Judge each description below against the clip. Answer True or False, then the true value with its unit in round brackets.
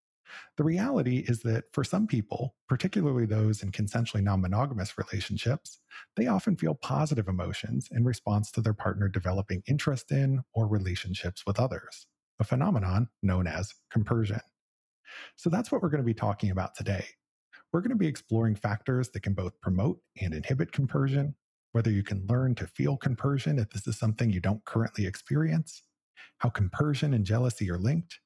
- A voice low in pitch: True (115 Hz)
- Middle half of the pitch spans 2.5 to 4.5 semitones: False (5.2 semitones)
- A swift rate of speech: False (170 wpm)